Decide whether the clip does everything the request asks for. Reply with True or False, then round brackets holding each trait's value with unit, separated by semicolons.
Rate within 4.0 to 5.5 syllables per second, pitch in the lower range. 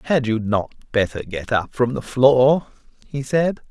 True (4.4 syllables/s; 125 Hz)